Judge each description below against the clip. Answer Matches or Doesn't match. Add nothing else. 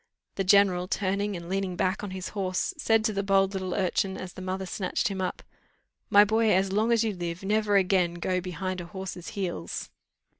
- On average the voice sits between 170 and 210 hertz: Matches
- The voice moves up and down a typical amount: Doesn't match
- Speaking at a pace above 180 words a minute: Matches